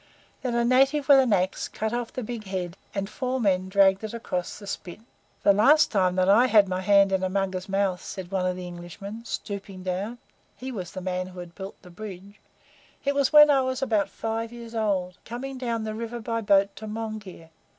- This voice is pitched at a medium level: No, high, 205 Hz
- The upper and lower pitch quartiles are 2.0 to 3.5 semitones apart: No, average, 3.9 semitones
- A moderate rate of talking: No, fast, 215 wpm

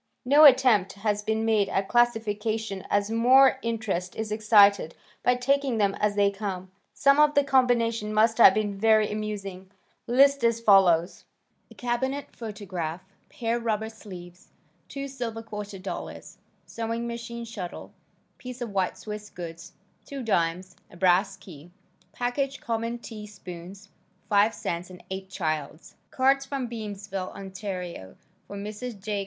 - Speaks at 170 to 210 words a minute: No, average, 145 wpm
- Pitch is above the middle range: Yes, high, 215 Hz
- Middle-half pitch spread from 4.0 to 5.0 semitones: No, average, 3.4 semitones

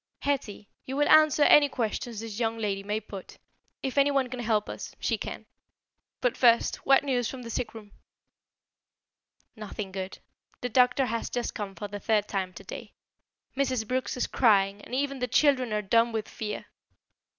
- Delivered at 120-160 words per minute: No, average, 175 wpm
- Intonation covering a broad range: No, average, 3.7 semitones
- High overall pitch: Yes, high, 230 Hz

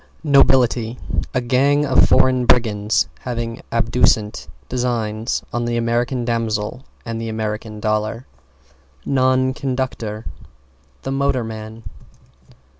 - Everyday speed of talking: No, slow, 100 wpm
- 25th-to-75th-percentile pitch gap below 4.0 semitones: Yes, average, 2.7 semitones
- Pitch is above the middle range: No, low, 115 Hz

